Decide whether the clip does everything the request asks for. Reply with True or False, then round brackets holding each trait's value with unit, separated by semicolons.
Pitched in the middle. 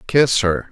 False (115 Hz)